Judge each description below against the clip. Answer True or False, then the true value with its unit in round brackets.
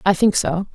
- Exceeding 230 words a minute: True (240 wpm)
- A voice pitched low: False (185 Hz)